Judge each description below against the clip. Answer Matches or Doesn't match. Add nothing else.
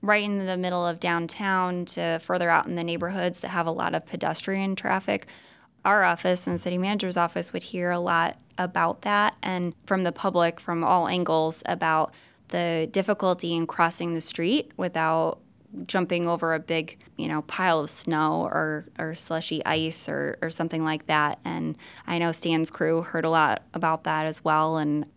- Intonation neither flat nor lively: Doesn't match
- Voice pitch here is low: Doesn't match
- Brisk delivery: Doesn't match